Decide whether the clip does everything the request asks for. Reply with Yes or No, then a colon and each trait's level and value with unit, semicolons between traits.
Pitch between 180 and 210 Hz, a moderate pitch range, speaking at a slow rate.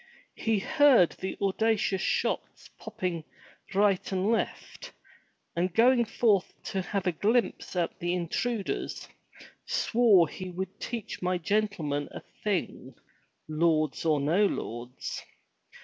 Yes: high, 190 Hz; average, 4.1 semitones; slow, 115 wpm